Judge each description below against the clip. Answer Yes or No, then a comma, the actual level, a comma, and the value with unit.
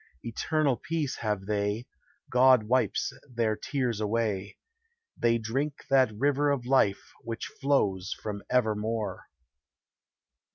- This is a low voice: Yes, low, 115 Hz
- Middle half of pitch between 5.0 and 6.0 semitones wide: No, average, 3.9 semitones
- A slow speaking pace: Yes, slow, 110 wpm